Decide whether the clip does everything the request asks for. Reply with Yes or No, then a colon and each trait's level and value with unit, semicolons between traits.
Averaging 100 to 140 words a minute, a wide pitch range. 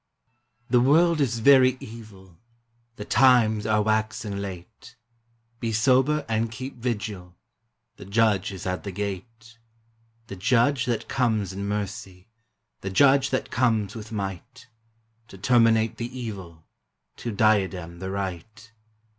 No: slow, 135 wpm; average, 3.5 semitones